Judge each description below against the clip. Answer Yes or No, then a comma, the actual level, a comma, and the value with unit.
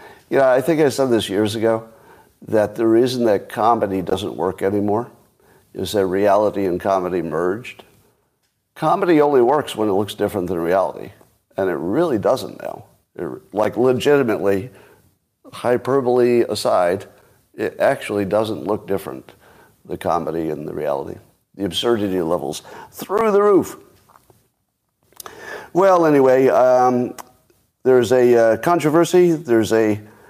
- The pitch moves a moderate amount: Yes, average, 4.5 semitones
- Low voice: Yes, low, 115 Hz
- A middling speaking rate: No, slow, 130 wpm